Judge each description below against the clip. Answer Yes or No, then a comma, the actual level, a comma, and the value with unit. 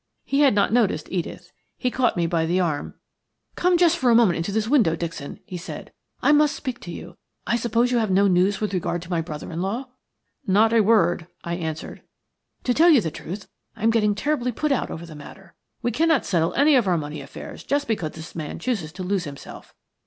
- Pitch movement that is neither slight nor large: No, wide, 6.3 semitones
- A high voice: Yes, high, 200 Hz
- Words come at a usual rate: No, fast, 225 wpm